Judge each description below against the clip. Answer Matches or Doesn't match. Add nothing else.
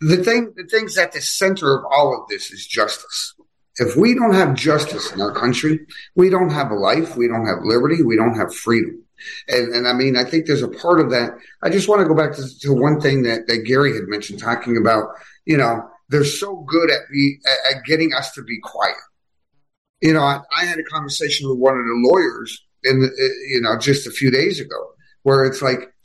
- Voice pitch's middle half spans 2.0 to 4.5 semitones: Doesn't match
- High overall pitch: Doesn't match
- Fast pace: Matches